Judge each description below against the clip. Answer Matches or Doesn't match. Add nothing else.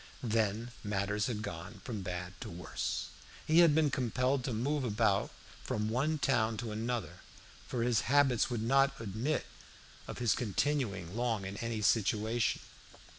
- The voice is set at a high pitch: Doesn't match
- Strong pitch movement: Doesn't match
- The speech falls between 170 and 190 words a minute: Doesn't match